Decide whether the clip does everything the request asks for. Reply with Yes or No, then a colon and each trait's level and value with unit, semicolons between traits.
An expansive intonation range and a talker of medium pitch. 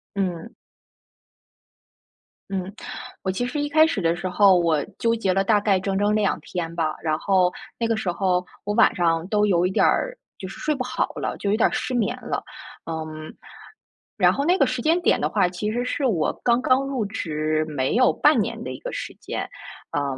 No: wide, 5.9 semitones; high, 200 Hz